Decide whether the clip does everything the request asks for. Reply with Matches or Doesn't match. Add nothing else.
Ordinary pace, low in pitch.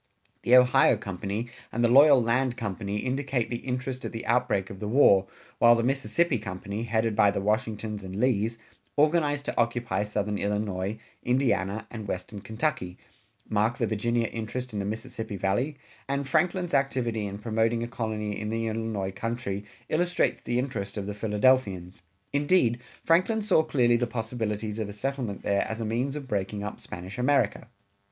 Matches